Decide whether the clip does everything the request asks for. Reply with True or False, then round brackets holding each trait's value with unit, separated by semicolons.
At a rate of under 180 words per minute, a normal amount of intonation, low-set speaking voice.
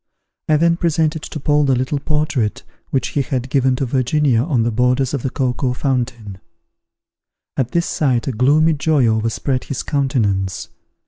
True (170 wpm; 3.5 semitones; 130 Hz)